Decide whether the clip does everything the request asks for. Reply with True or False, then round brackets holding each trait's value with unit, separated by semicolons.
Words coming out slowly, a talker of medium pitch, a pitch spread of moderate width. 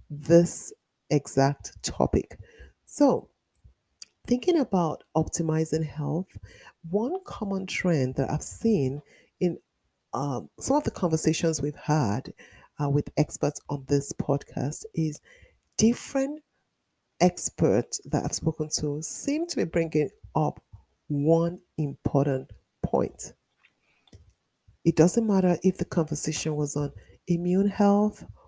True (110 wpm; 160 Hz; 4.6 semitones)